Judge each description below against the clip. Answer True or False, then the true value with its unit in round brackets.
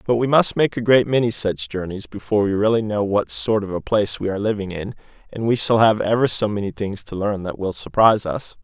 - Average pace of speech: False (250 wpm)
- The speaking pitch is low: True (105 Hz)